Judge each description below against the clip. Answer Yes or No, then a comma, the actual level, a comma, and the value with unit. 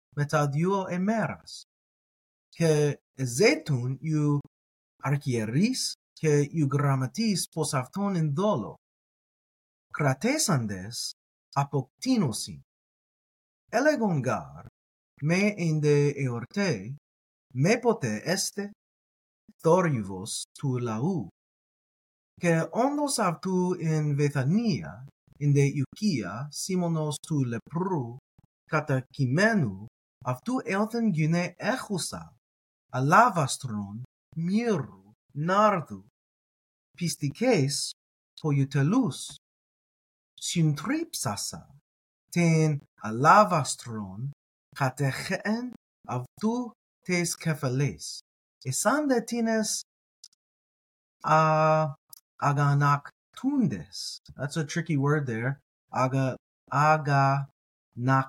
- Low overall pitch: No, medium, 150 Hz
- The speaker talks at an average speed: No, slow, 75 wpm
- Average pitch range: No, wide, 6.0 semitones